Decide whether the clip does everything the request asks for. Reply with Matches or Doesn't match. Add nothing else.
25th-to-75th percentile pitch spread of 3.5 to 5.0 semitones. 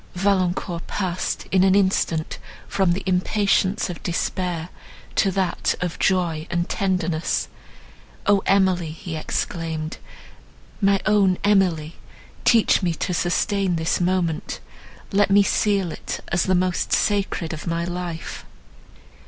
Doesn't match